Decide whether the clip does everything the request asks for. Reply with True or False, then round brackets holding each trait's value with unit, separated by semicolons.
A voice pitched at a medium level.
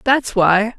False (215 Hz)